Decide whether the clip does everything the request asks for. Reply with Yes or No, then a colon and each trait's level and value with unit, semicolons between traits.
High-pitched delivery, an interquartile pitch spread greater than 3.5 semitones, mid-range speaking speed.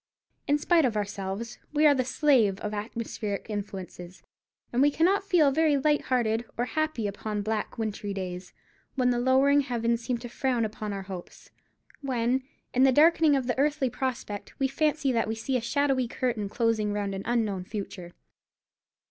Yes: high, 240 Hz; average, 4.8 semitones; average, 175 wpm